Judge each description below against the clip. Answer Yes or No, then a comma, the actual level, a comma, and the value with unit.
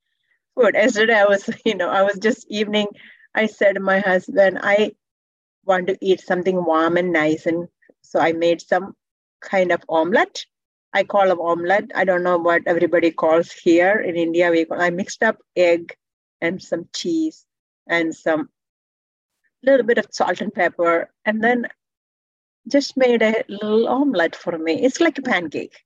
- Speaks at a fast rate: No, average, 165 wpm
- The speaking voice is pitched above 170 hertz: Yes, high, 190 Hz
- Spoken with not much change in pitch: No, average, 4.3 semitones